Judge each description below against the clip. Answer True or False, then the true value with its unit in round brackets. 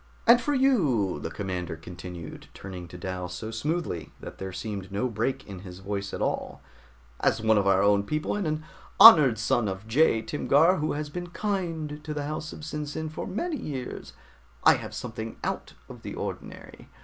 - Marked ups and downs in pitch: True (8.1 semitones)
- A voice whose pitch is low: True (115 Hz)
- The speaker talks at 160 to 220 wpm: True (185 wpm)